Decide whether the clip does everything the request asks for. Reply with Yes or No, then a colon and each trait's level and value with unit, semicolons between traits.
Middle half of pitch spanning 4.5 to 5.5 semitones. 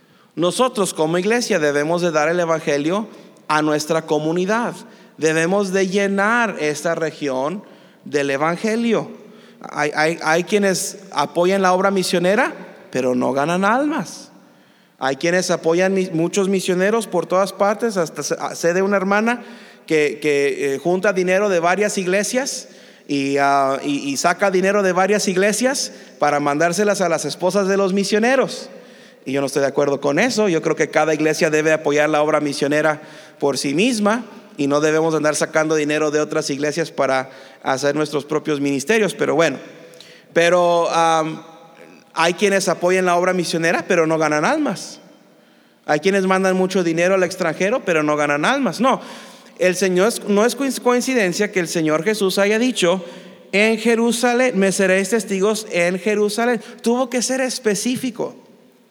Yes: average, 5.2 semitones